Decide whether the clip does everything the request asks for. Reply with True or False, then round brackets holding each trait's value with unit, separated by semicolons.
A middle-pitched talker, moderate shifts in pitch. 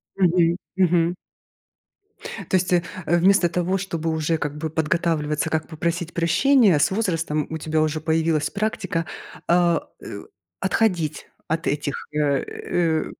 False (165 Hz; 2.2 semitones)